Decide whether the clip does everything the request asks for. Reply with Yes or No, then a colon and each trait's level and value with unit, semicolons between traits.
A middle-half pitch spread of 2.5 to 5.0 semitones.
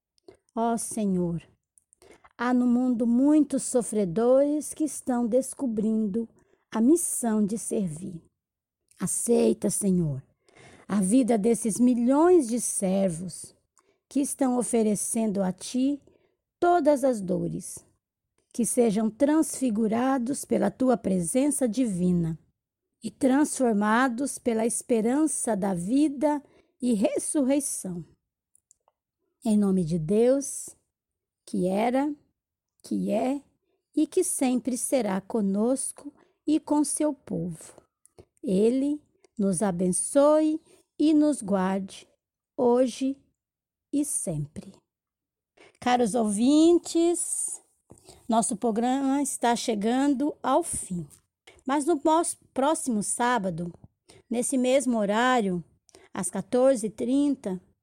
No: wide, 5.6 semitones